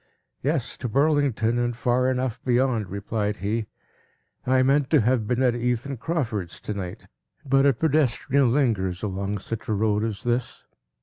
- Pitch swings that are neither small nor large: Yes, average, 3.7 semitones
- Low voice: Yes, low, 120 Hz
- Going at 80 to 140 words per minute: No, average, 160 wpm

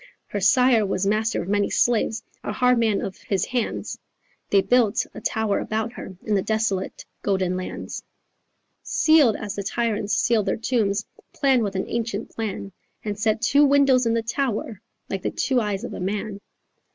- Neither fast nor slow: Yes, average, 175 wpm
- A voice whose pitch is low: No, high, 220 Hz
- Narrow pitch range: No, average, 3.0 semitones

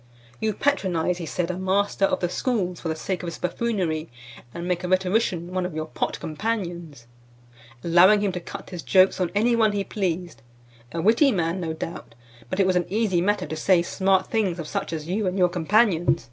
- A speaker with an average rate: No, fast, 210 wpm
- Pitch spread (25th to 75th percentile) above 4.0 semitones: No, average, 2.9 semitones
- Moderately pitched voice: Yes, medium, 180 Hz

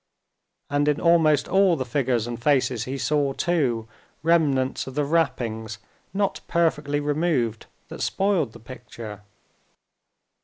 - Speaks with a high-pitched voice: No, medium, 140 Hz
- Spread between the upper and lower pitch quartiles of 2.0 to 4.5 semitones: No, average, 5.0 semitones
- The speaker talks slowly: Yes, slow, 125 wpm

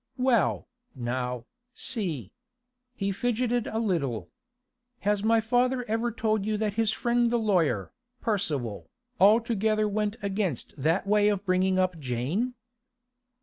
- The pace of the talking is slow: Yes, slow, 125 wpm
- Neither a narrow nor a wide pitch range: Yes, average, 5.0 semitones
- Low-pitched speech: No, high, 210 Hz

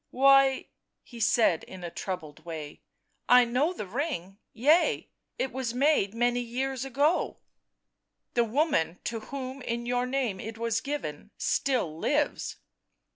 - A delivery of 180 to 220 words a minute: No, average, 160 wpm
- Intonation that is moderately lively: Yes, average, 4.9 semitones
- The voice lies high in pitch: Yes, high, 245 Hz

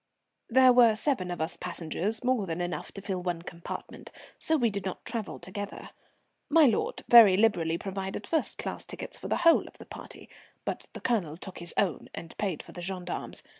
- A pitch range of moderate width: Yes, average, 4.6 semitones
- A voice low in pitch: No, high, 195 Hz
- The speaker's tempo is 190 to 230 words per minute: Yes, average, 195 wpm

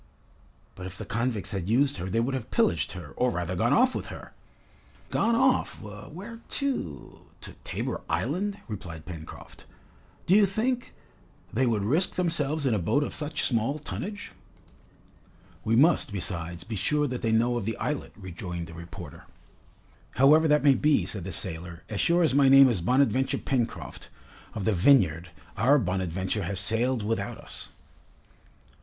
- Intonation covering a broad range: Yes, wide, 7.9 semitones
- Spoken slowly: No, average, 165 wpm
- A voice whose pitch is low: Yes, low, 115 Hz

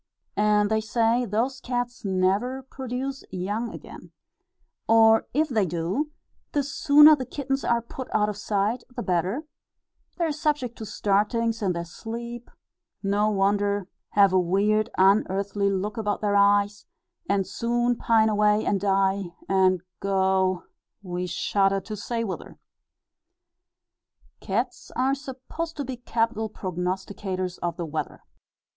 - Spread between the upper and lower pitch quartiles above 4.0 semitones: No, average, 3.7 semitones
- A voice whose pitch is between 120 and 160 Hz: No, high, 210 Hz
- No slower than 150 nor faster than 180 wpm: No, slow, 135 wpm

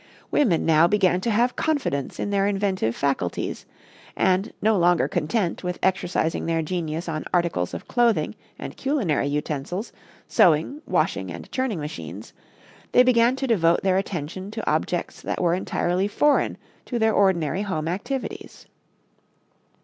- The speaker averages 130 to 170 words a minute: Yes, average, 140 wpm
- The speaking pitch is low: No, medium, 185 Hz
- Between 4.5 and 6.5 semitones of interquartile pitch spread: Yes, average, 5.3 semitones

